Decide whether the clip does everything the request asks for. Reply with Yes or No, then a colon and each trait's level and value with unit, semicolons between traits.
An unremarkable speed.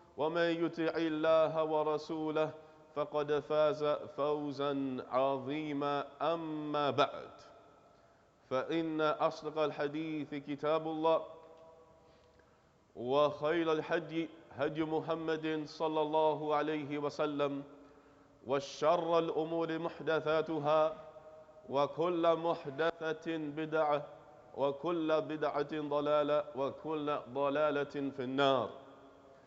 No: slow, 75 wpm